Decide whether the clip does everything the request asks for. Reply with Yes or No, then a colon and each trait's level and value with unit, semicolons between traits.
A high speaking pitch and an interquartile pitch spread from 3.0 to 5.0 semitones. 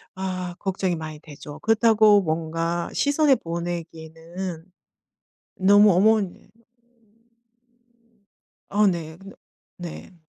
No: medium, 180 Hz; average, 3.6 semitones